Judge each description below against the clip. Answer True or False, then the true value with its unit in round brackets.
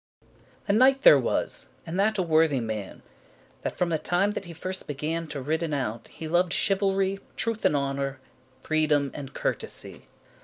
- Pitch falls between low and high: True (160 Hz)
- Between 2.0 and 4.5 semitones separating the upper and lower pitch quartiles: False (5.3 semitones)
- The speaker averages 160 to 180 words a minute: True (165 wpm)